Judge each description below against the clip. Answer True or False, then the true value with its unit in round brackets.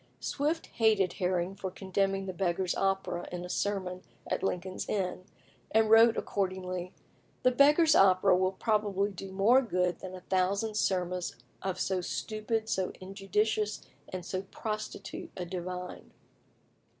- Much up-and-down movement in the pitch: False (2.5 semitones)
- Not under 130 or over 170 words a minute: True (140 wpm)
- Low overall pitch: False (190 Hz)